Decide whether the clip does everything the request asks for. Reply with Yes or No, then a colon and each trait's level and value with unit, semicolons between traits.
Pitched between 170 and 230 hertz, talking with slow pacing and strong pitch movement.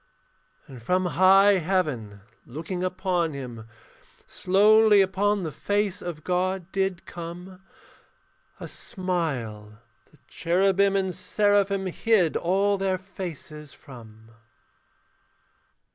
No: medium, 185 Hz; slow, 100 wpm; average, 3.9 semitones